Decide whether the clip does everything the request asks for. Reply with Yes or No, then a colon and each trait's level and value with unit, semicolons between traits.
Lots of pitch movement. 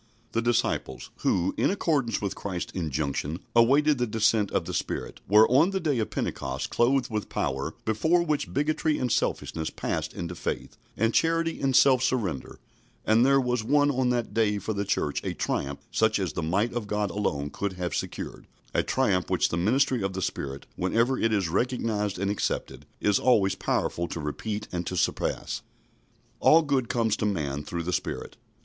Yes: wide, 5.9 semitones